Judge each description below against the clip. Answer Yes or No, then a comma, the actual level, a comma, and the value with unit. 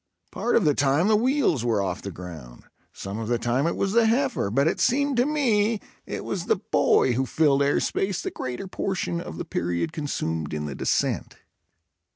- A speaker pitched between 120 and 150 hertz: Yes, medium, 140 Hz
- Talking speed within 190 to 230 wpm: Yes, average, 200 wpm